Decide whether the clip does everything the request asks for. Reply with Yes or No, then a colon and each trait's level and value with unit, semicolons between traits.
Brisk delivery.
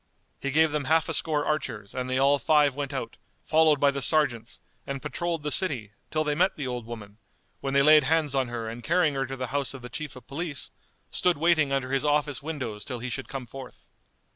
Yes: fast, 230 wpm